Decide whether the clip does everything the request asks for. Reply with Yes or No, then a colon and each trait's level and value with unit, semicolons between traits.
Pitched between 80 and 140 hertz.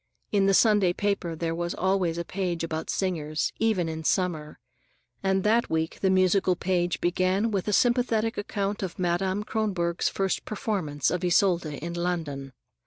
No: medium, 185 Hz